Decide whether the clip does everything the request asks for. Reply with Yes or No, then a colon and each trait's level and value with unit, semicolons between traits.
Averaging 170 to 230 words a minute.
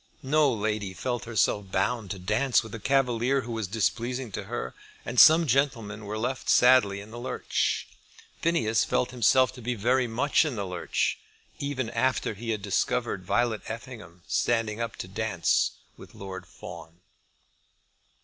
No: average, 160 wpm